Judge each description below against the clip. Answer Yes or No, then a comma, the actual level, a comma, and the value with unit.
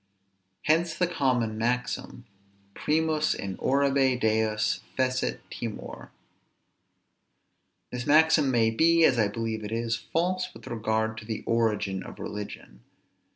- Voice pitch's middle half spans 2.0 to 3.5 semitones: No, wide, 5.5 semitones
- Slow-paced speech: Yes, slow, 120 wpm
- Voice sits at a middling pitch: No, low, 120 Hz